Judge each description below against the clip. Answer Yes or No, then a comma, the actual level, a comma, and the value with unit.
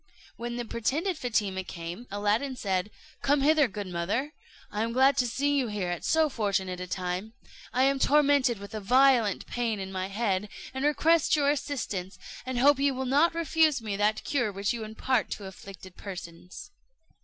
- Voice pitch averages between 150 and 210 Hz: No, high, 230 Hz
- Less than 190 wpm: Yes, average, 180 wpm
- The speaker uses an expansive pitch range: Yes, wide, 5.8 semitones